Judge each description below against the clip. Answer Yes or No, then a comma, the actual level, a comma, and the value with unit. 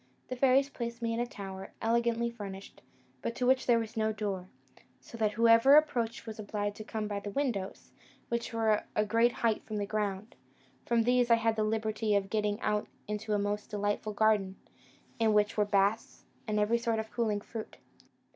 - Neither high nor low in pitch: No, high, 220 Hz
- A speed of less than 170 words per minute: No, average, 190 wpm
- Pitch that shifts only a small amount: Yes, narrow, 2.1 semitones